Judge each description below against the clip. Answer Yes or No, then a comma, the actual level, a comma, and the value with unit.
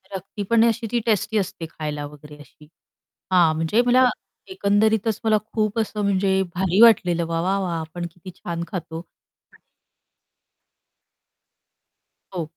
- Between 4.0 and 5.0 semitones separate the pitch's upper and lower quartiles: Yes, average, 4.5 semitones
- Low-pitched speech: No, high, 190 Hz